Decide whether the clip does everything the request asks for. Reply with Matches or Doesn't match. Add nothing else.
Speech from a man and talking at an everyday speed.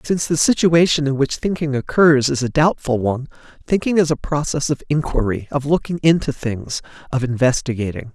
Matches